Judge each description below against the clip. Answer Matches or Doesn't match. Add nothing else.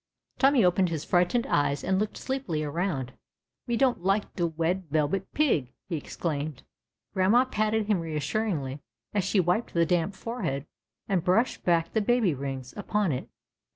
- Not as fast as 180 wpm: Matches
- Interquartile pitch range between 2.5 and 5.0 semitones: Doesn't match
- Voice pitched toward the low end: Doesn't match